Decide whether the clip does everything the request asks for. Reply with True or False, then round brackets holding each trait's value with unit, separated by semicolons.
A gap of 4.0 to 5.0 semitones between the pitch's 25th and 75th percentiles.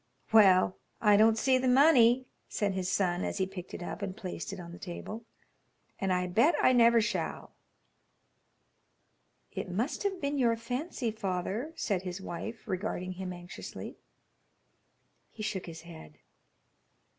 True (4.3 semitones)